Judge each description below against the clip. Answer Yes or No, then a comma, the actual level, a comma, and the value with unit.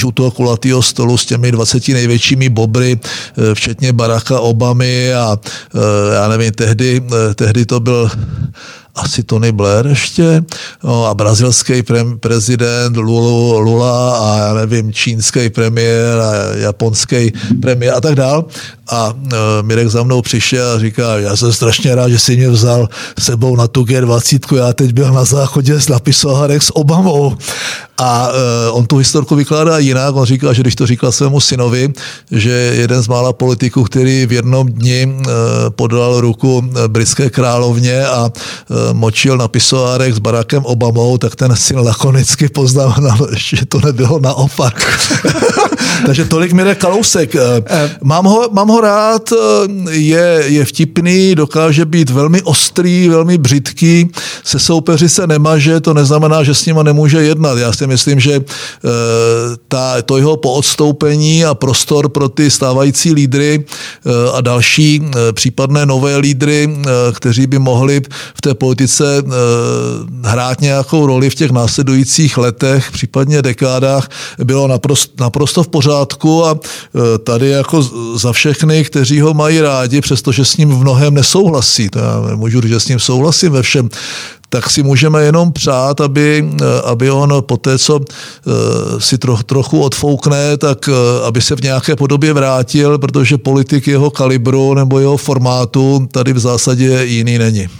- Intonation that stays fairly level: No, average, 3.4 semitones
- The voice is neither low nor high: No, low, 130 Hz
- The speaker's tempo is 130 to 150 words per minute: Yes, average, 145 wpm